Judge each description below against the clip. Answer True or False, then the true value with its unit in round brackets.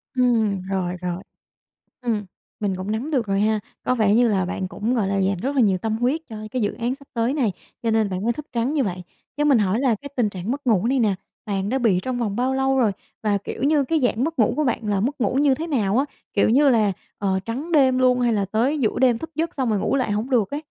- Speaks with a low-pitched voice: False (230 Hz)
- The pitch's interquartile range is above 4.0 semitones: True (4.5 semitones)